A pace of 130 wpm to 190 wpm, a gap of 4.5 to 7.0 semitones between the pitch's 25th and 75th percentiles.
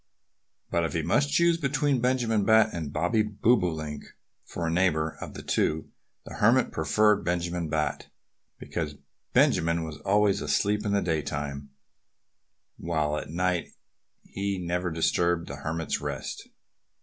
Yes: slow, 135 wpm; average, 4.9 semitones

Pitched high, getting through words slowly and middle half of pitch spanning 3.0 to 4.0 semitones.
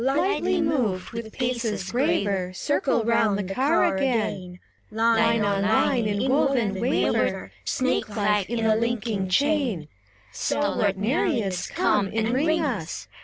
No: high, 225 Hz; slow, 125 wpm; average, 4.7 semitones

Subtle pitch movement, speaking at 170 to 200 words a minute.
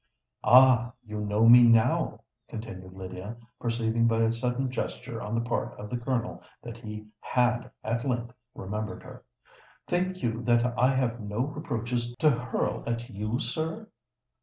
No: narrow, 1.9 semitones; average, 155 wpm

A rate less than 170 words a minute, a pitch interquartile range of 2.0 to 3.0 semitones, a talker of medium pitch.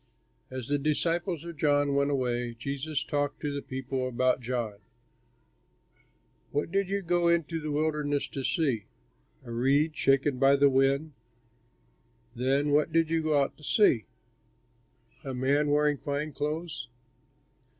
Yes: average, 140 wpm; average, 2.7 semitones; medium, 145 Hz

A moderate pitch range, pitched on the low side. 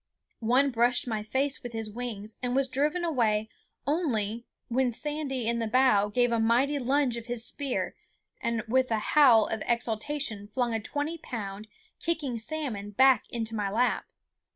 No: average, 3.5 semitones; high, 240 Hz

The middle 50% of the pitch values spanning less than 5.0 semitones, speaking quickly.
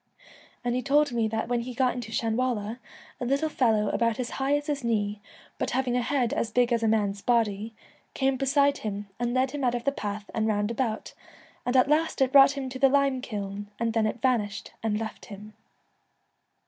Yes: average, 3.5 semitones; fast, 210 wpm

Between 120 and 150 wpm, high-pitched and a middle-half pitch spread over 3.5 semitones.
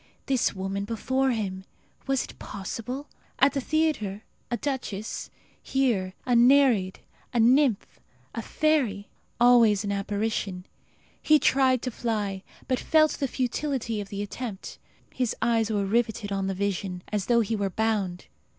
Yes: average, 145 wpm; high, 225 Hz; average, 4.4 semitones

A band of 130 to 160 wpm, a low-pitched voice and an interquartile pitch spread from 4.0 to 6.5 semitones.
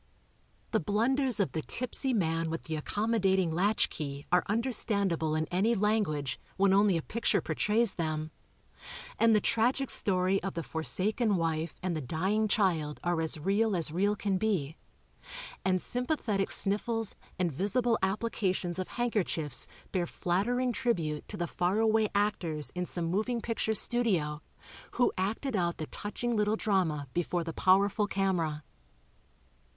No: average, 150 wpm; high, 195 Hz; average, 4.8 semitones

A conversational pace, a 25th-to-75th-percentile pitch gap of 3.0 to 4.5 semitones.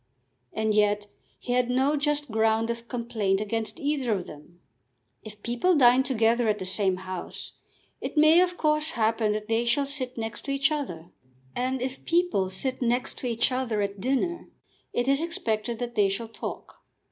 Yes: average, 180 wpm; average, 4.2 semitones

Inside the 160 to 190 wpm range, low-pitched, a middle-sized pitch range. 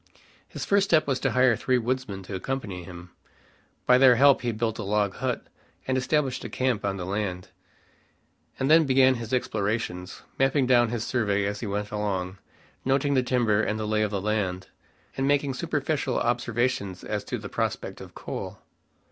Yes: average, 180 wpm; low, 115 Hz; average, 4.3 semitones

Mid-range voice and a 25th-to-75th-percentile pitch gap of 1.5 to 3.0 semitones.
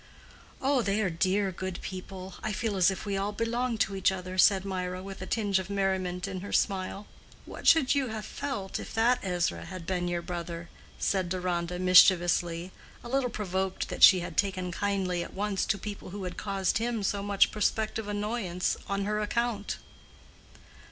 No: high, 195 Hz; narrow, 2.4 semitones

